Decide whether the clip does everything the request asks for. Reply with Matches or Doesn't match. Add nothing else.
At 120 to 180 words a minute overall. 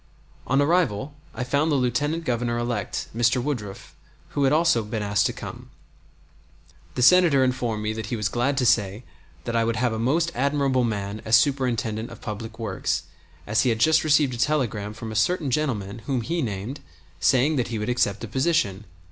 Doesn't match